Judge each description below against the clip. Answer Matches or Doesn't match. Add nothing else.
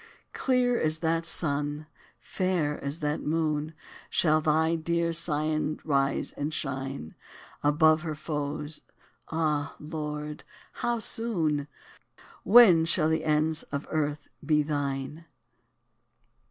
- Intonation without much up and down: Matches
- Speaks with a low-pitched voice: Doesn't match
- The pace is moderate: Doesn't match